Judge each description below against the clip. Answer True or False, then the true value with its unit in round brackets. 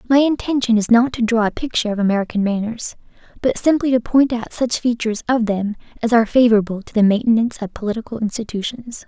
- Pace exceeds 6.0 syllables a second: True (6.5 syllables/s)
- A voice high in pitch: True (230 Hz)